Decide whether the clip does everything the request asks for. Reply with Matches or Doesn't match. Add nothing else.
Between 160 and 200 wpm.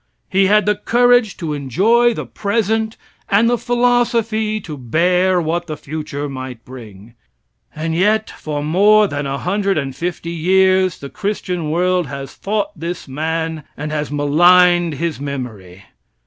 Doesn't match